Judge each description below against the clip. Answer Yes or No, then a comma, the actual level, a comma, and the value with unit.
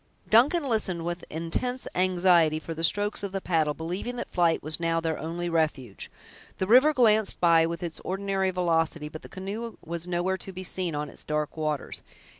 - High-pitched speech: No, medium, 175 Hz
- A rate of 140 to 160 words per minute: No, average, 190 wpm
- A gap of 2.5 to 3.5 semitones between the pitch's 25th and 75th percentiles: Yes, average, 3.1 semitones